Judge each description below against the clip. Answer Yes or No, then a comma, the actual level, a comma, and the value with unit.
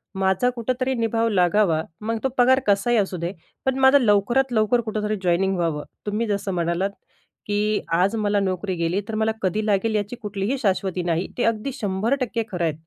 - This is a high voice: Yes, high, 210 Hz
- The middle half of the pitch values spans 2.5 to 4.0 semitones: Yes, average, 3.3 semitones